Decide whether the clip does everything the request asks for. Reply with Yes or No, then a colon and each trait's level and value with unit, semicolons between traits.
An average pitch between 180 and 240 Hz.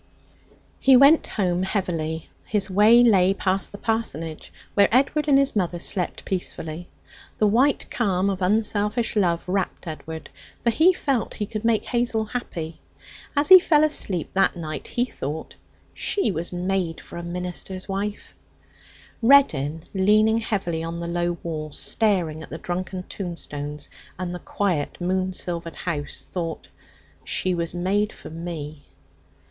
Yes: medium, 185 Hz